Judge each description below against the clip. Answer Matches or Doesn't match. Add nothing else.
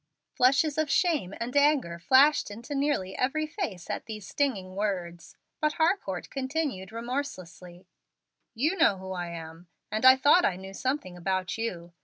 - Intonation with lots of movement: Matches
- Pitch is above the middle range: Matches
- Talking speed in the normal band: Matches